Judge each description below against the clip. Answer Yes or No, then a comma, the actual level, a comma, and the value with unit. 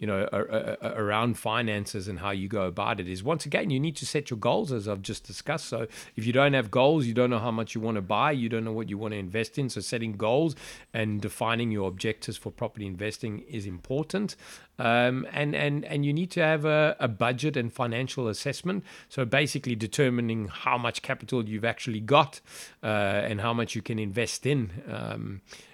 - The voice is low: Yes, low, 115 Hz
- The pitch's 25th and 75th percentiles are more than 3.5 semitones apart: Yes, average, 3.9 semitones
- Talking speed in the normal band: No, fast, 210 wpm